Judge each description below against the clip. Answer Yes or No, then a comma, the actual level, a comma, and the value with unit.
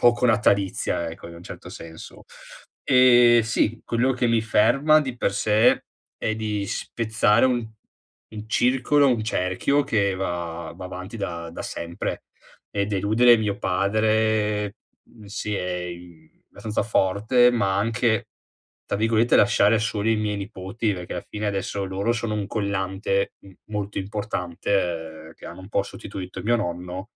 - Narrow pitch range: No, average, 3.3 semitones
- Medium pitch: No, low, 105 Hz